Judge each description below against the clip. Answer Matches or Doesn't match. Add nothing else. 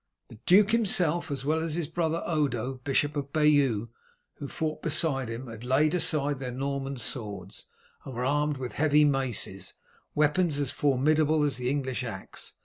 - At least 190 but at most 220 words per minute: Doesn't match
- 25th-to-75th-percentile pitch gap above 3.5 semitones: Doesn't match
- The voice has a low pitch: Doesn't match